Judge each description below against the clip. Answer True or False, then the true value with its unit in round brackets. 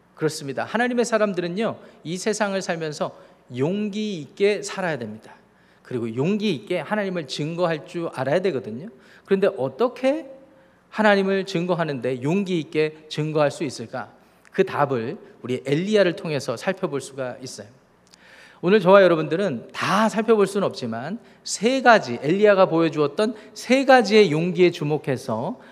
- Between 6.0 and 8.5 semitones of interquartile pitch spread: False (5.6 semitones)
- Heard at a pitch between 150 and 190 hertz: True (185 Hz)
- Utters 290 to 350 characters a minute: True (325 characters per minute)